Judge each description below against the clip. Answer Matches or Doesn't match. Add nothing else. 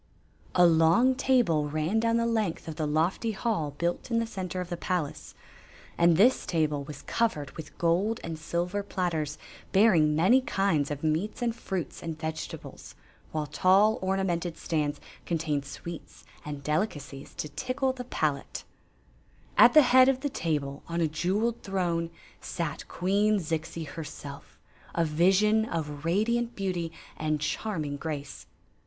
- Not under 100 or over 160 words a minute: Matches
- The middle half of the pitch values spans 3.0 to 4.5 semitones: Doesn't match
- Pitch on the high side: Doesn't match